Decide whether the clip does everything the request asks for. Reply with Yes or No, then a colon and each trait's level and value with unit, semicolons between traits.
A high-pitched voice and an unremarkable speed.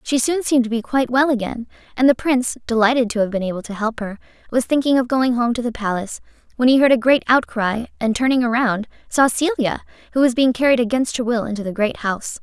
No: high, 240 Hz; fast, 235 wpm